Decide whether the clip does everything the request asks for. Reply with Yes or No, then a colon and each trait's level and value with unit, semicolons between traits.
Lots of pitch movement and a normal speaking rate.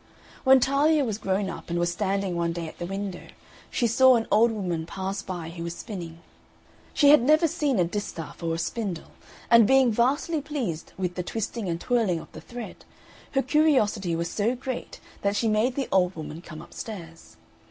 Yes: wide, 6.2 semitones; average, 195 wpm